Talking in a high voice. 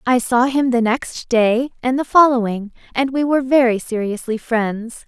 Yes: high, 245 Hz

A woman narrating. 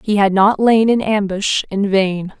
Yes: female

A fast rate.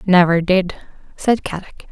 No: slow, 125 wpm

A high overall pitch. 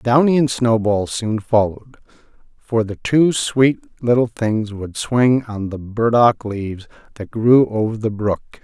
No: low, 115 Hz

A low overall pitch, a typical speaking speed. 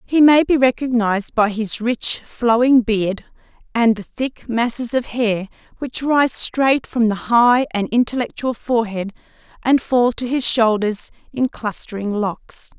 No: high, 235 Hz; average, 150 wpm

